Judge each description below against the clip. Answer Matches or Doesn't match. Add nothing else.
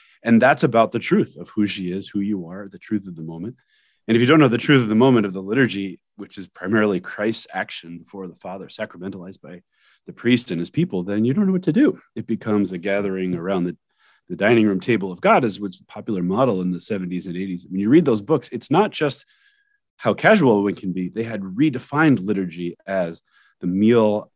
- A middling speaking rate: Doesn't match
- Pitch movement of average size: Matches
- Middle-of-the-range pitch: Doesn't match